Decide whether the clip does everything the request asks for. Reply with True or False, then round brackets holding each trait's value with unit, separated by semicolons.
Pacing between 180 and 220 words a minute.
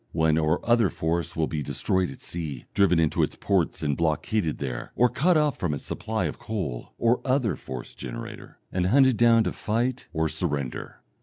True (185 wpm)